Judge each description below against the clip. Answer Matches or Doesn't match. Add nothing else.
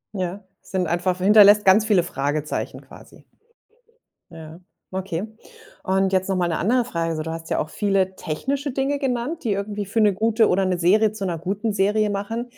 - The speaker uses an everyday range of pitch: Matches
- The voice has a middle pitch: Doesn't match